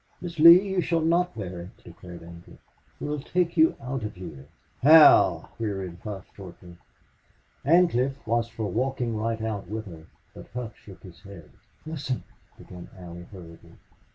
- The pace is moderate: Yes, average, 155 wpm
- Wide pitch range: Yes, wide, 8.5 semitones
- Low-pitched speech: Yes, low, 110 Hz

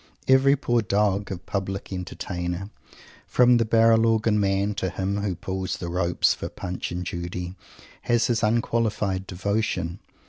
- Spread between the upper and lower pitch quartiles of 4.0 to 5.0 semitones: No, average, 3.6 semitones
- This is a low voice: Yes, low, 100 Hz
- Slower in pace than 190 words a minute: Yes, average, 145 wpm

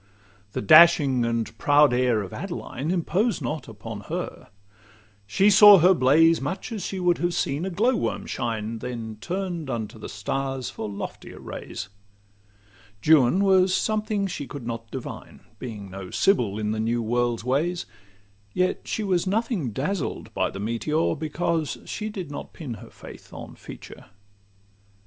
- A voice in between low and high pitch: Yes, medium, 145 Hz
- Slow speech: No, average, 155 wpm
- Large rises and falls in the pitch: Yes, wide, 7.9 semitones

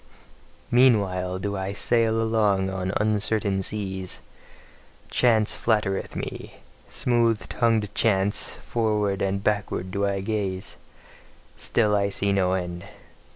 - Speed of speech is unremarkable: No, slow, 110 wpm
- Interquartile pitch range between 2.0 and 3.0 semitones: Yes, narrow, 2.4 semitones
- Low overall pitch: Yes, low, 100 Hz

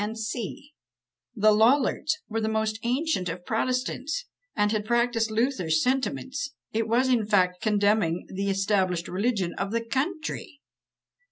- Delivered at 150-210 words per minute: No, slow, 135 wpm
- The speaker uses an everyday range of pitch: Yes, average, 4.2 semitones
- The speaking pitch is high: Yes, high, 220 Hz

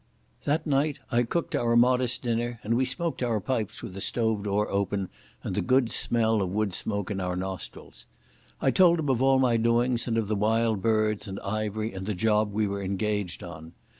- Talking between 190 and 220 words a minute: Yes, average, 200 wpm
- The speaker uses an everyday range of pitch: Yes, average, 3.3 semitones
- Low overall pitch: Yes, low, 110 Hz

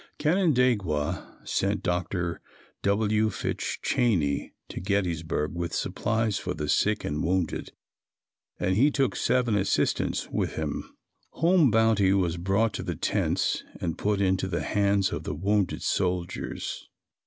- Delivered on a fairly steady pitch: No, average, 4.0 semitones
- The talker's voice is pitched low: Yes, low, 100 Hz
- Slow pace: Yes, slow, 130 wpm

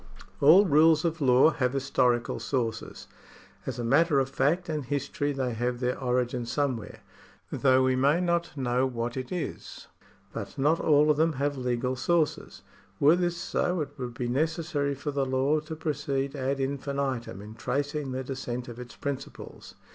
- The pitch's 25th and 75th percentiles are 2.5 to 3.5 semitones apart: Yes, average, 3.1 semitones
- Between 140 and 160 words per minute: No, average, 170 wpm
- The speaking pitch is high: No, low, 135 Hz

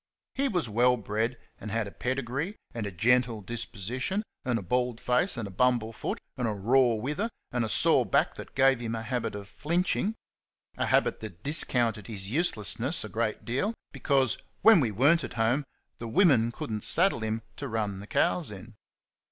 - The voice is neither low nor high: No, low, 120 Hz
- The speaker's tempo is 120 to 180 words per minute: No, average, 195 wpm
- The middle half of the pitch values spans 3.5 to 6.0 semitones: Yes, average, 3.8 semitones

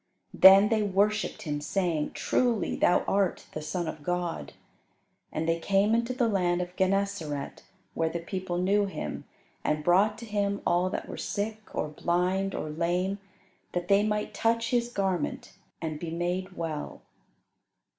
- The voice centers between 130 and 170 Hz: No, medium, 185 Hz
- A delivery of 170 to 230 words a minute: No, average, 155 wpm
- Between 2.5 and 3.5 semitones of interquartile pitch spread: Yes, average, 3.2 semitones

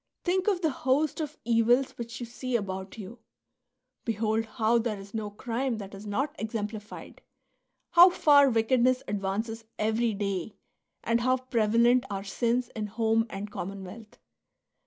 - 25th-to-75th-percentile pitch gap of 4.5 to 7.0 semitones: No, average, 3.3 semitones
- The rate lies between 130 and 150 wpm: Yes, average, 145 wpm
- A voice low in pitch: No, high, 230 Hz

